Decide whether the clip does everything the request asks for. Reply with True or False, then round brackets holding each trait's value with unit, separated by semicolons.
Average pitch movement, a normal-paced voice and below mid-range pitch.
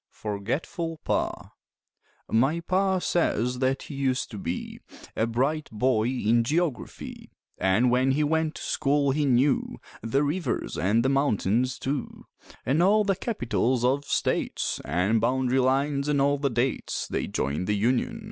True (4.0 semitones; 150 wpm; 130 Hz)